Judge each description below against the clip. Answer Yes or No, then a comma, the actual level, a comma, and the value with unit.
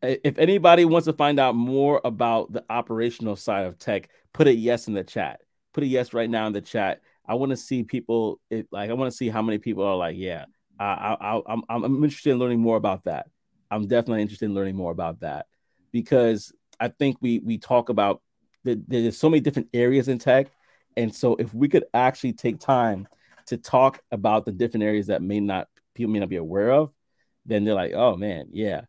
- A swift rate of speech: Yes, fast, 220 wpm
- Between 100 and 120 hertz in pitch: Yes, low, 115 Hz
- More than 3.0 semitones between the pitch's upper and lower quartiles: Yes, average, 3.4 semitones